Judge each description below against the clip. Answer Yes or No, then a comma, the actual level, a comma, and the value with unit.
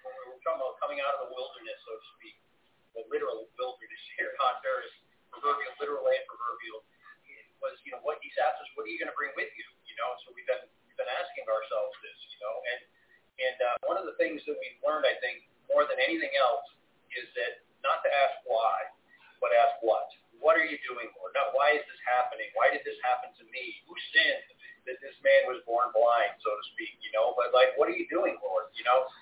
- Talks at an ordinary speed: No, fast, 230 wpm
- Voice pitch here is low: No, very high, 330 Hz